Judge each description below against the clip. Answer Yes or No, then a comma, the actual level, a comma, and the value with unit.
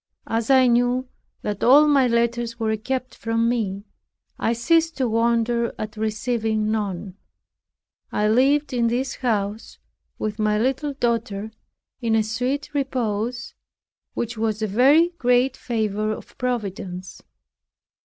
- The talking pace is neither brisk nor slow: No, slow, 130 wpm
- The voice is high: Yes, high, 235 Hz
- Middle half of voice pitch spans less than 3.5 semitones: Yes, average, 2.8 semitones